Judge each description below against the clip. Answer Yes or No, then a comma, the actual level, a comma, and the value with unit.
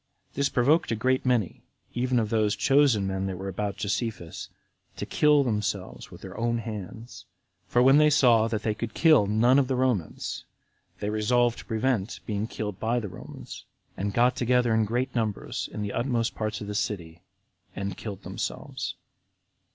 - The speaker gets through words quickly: No, average, 175 wpm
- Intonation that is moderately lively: Yes, average, 3.2 semitones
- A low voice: Yes, low, 115 Hz